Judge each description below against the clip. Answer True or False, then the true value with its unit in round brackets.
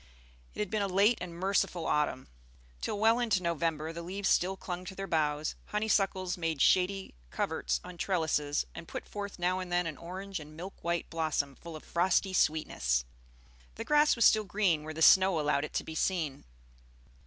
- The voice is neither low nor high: True (175 Hz)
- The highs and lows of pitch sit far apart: False (3.6 semitones)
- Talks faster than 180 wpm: True (190 wpm)